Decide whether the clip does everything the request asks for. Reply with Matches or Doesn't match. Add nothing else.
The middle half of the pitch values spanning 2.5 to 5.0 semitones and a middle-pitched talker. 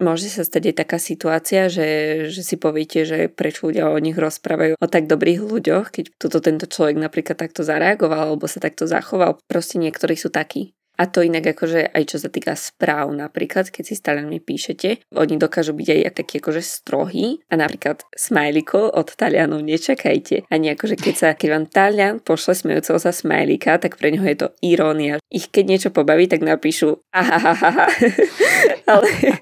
Matches